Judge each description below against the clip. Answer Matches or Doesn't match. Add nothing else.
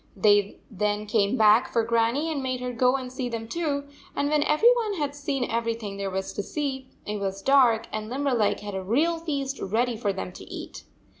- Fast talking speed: Matches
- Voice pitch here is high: Matches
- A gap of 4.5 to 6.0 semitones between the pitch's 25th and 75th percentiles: Matches